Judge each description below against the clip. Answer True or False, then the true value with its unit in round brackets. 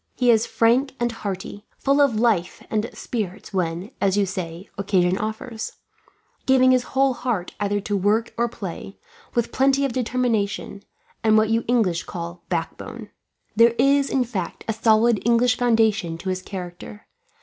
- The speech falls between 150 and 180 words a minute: True (160 wpm)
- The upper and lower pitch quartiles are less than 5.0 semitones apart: True (3.8 semitones)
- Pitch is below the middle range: False (220 Hz)